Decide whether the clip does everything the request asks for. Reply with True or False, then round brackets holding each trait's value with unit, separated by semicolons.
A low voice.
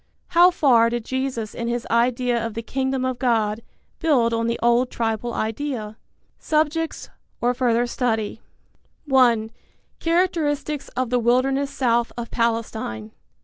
False (240 Hz)